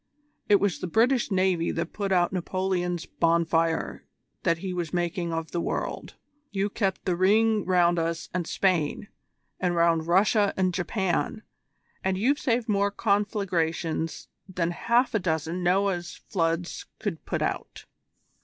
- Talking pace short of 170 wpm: Yes, average, 145 wpm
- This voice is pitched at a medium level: Yes, medium, 180 Hz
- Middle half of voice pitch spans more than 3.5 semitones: No, average, 2.9 semitones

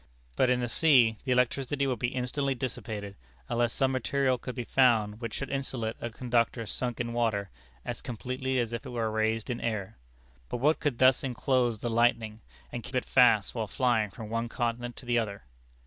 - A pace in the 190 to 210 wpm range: Yes, average, 195 wpm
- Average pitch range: No, narrow, 2.3 semitones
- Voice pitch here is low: Yes, low, 120 Hz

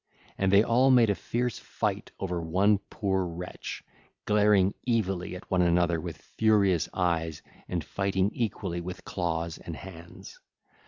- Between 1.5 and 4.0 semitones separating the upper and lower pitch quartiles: Yes, average, 3.0 semitones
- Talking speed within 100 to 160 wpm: Yes, average, 145 wpm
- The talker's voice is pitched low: Yes, very low, 95 Hz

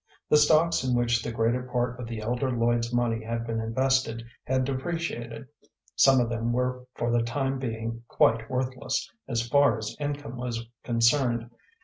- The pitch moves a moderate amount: No, narrow, 2.1 semitones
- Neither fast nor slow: Yes, average, 165 wpm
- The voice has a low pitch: Yes, low, 120 Hz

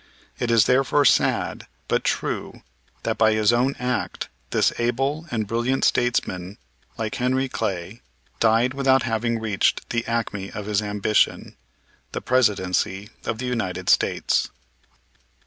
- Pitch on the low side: Yes, low, 115 Hz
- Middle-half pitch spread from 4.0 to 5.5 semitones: No, average, 3.3 semitones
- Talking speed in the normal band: No, slow, 130 wpm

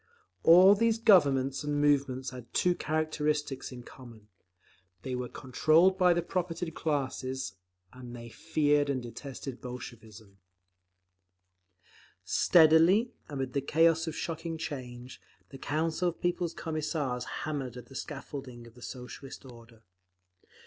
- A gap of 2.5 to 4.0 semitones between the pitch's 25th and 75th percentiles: No, average, 4.4 semitones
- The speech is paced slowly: Yes, slow, 125 wpm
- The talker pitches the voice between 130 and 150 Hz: Yes, medium, 140 Hz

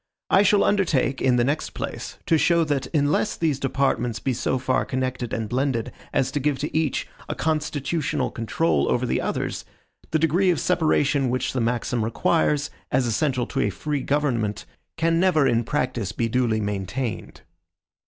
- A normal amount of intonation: Yes, average, 4.1 semitones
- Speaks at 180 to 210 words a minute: No, average, 170 wpm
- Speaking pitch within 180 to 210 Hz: No, low, 135 Hz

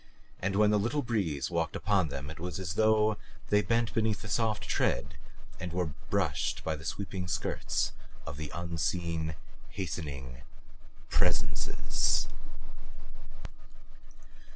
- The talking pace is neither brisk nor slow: No, slow, 120 wpm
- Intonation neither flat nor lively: Yes, average, 4.9 semitones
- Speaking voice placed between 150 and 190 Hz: No, very low, 90 Hz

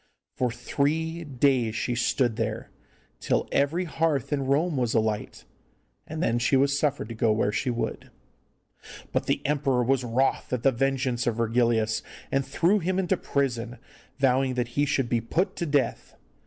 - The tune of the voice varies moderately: Yes, average, 3.5 semitones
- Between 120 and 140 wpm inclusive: No, average, 170 wpm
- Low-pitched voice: Yes, low, 130 Hz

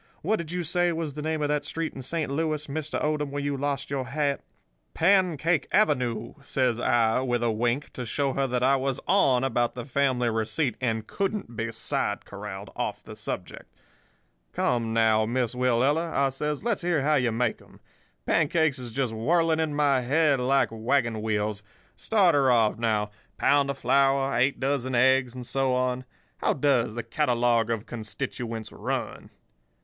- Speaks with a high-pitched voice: No, low, 130 Hz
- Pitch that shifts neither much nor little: Yes, average, 3.9 semitones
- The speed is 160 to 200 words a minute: Yes, average, 175 wpm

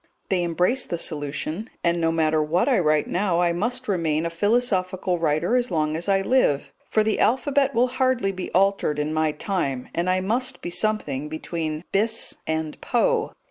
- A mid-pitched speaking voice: Yes, medium, 180 Hz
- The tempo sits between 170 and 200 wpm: Yes, average, 180 wpm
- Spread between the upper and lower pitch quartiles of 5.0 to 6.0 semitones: Yes, wide, 5.5 semitones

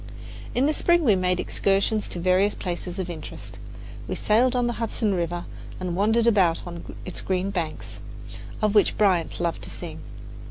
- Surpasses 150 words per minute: Yes, average, 170 wpm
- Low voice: No, high, 190 Hz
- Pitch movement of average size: Yes, average, 3.8 semitones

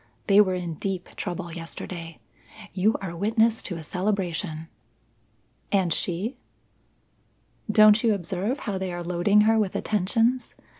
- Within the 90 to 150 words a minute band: Yes, slow, 135 wpm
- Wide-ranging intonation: No, average, 3.5 semitones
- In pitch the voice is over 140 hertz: Yes, high, 190 Hz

